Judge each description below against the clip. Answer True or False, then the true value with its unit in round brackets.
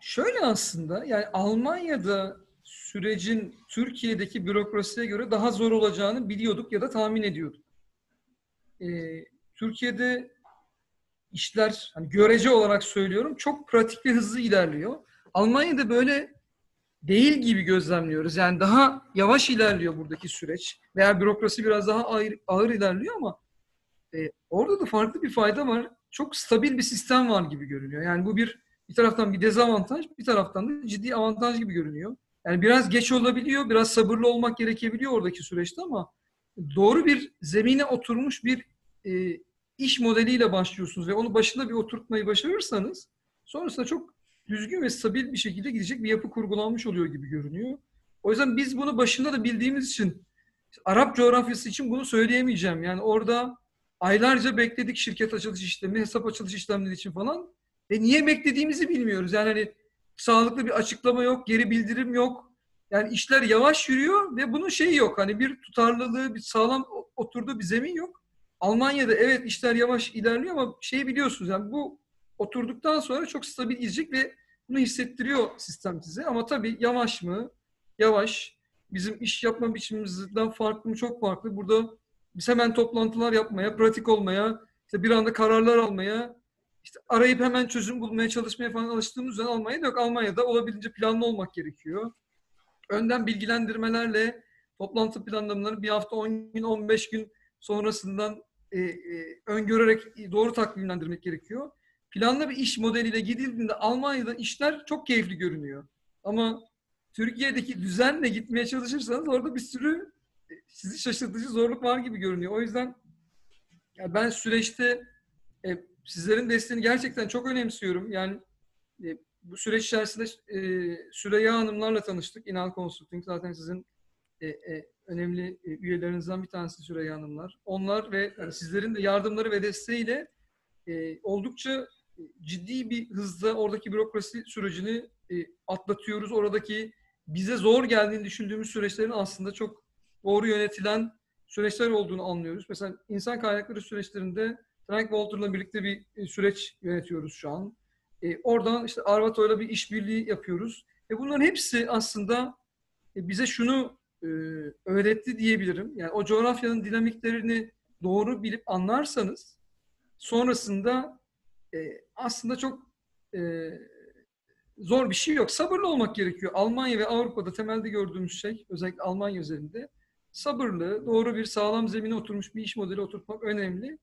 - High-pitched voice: True (220 Hz)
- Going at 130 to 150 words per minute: True (135 wpm)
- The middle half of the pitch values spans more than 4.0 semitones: False (3.4 semitones)